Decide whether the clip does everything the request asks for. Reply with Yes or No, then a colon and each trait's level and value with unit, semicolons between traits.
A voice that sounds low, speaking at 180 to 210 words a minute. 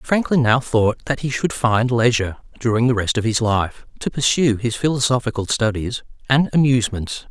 No: low, 120 Hz; average, 170 wpm